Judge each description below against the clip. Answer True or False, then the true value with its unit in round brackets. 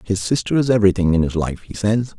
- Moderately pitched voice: False (100 Hz)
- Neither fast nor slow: False (245 wpm)